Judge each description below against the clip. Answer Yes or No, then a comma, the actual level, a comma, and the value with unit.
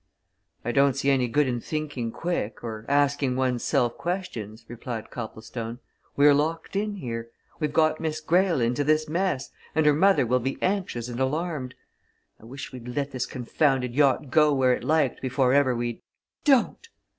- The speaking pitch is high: No, low, 135 Hz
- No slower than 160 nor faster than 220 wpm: Yes, average, 175 wpm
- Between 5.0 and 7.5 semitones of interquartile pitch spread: No, average, 4.2 semitones